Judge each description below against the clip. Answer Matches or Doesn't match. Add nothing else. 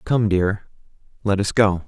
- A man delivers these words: Matches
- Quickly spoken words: Doesn't match